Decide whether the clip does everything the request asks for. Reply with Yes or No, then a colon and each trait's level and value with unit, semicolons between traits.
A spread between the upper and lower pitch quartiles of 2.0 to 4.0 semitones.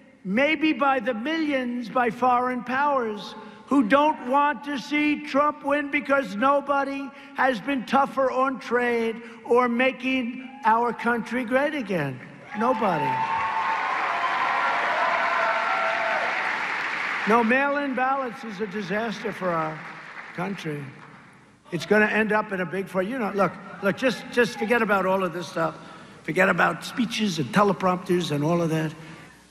No: wide, 5.6 semitones